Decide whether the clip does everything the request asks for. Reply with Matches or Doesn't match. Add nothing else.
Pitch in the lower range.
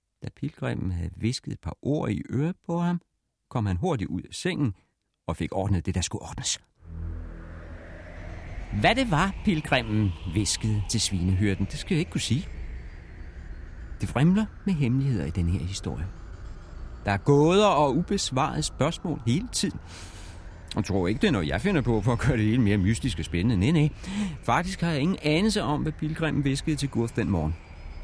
Matches